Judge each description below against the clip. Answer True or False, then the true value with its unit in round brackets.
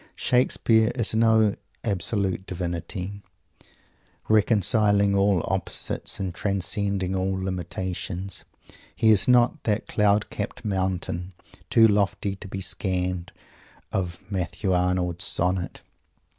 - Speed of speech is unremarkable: False (105 wpm)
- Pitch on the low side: True (95 Hz)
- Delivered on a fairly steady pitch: True (2.3 semitones)